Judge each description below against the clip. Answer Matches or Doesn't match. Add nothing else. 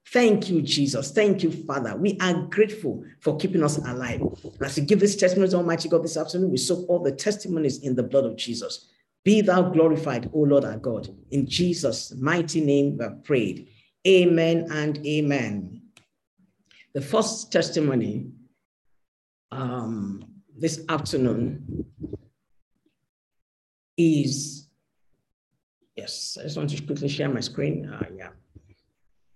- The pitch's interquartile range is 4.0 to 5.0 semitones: Matches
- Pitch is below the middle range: Doesn't match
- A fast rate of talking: Doesn't match